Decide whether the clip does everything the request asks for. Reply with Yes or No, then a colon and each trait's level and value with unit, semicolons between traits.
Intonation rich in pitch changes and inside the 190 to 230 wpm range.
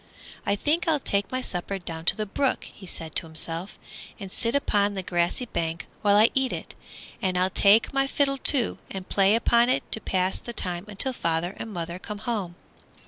No: average, 4.9 semitones; average, 200 wpm